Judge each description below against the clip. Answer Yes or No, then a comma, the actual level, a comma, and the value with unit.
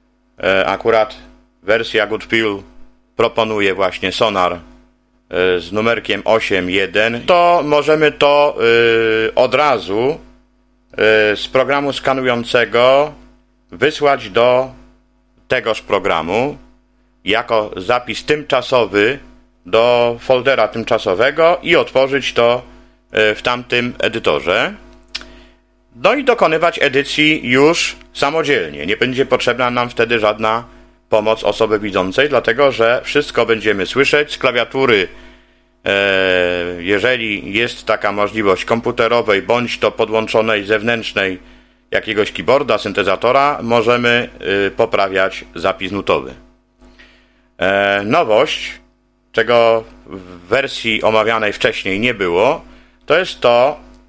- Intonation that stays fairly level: No, average, 3.2 semitones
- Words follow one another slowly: Yes, slow, 95 wpm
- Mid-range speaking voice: No, low, 115 Hz